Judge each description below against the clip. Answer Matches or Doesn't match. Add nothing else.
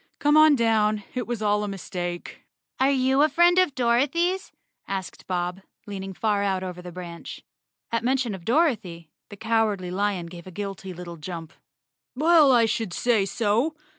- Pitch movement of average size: Doesn't match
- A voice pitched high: Matches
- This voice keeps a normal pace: Matches